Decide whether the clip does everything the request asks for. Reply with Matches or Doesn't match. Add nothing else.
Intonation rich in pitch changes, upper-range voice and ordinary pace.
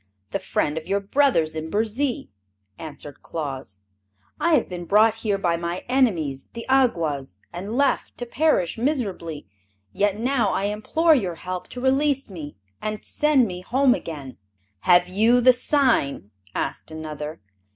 Matches